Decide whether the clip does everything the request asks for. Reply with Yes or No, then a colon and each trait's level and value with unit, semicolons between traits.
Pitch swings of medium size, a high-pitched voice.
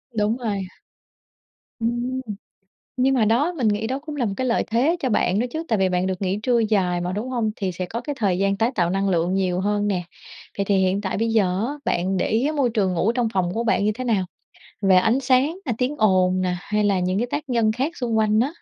Yes: average, 4.6 semitones; high, 215 Hz